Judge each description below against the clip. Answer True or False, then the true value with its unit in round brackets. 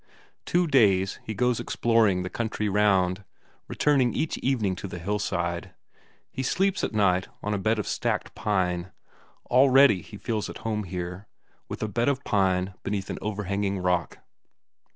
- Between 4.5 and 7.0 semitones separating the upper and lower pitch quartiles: False (4.0 semitones)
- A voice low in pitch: True (105 Hz)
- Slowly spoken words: False (155 wpm)